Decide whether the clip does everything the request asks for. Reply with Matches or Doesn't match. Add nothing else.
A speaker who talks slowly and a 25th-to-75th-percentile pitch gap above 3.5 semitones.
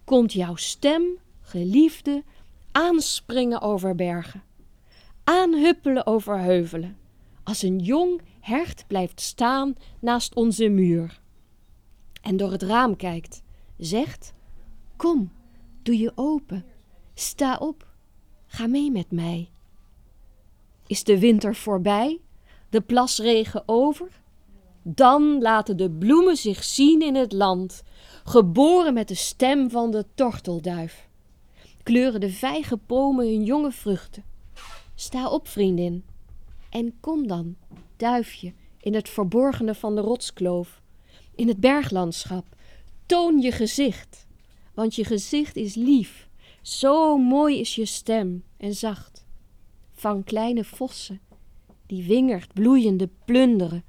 Matches